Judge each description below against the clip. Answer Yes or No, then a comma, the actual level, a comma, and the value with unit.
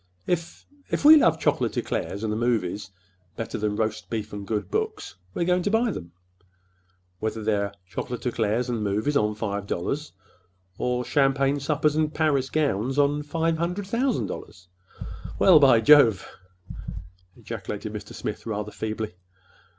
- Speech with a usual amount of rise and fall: No, wide, 6.2 semitones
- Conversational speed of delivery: Yes, average, 145 wpm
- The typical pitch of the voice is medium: No, low, 125 Hz